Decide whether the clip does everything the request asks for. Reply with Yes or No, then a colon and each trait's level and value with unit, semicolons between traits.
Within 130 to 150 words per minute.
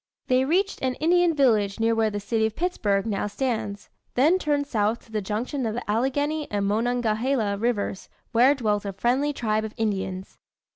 No: average, 180 wpm